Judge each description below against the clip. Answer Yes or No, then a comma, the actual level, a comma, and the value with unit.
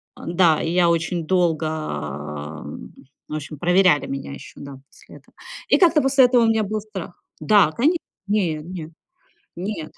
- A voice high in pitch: No, medium, 175 Hz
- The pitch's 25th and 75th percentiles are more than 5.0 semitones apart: Yes, wide, 5.4 semitones